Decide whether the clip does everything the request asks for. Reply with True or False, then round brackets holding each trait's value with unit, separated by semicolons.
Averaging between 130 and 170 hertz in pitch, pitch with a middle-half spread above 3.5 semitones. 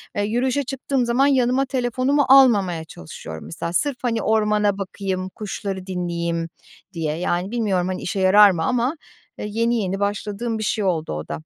False (205 Hz; 5.0 semitones)